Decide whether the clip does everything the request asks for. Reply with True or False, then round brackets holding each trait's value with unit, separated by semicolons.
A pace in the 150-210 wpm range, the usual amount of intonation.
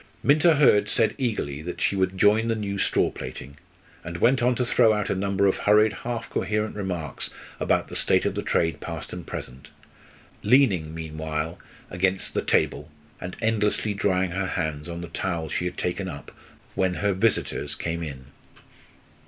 True (175 wpm; 4.3 semitones)